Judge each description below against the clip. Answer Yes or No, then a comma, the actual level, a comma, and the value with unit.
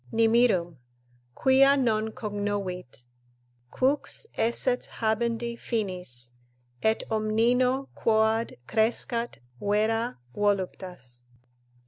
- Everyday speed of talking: No, slow, 70 wpm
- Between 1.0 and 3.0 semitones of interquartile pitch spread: Yes, narrow, 2.6 semitones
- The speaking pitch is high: Yes, high, 220 Hz